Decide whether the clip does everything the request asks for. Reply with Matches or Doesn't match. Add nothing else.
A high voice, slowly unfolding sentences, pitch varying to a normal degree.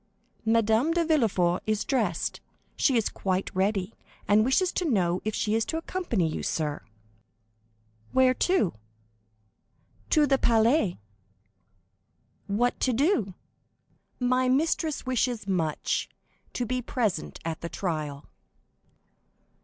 Doesn't match